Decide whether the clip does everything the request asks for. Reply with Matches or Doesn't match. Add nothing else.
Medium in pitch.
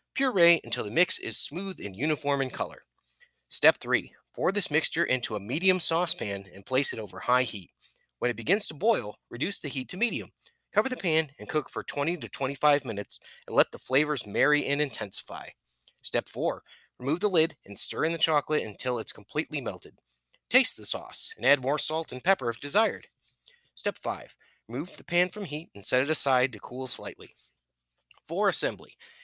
Matches